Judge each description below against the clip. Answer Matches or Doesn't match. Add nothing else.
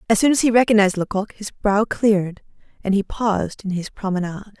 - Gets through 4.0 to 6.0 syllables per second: Doesn't match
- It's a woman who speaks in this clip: Matches